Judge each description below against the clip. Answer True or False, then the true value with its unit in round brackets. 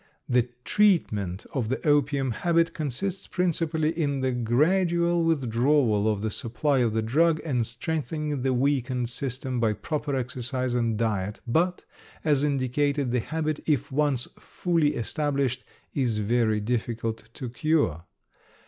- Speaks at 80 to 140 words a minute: True (135 wpm)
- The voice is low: True (130 Hz)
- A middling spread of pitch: True (4.6 semitones)